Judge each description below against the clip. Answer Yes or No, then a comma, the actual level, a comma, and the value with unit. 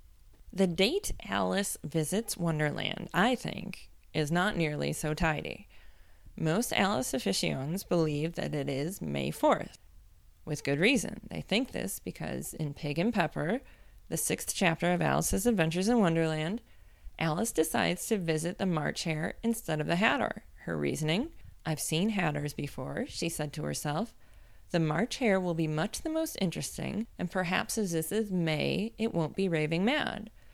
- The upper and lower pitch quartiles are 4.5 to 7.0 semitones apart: Yes, wide, 5.5 semitones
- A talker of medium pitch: Yes, medium, 170 Hz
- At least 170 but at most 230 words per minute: No, average, 160 wpm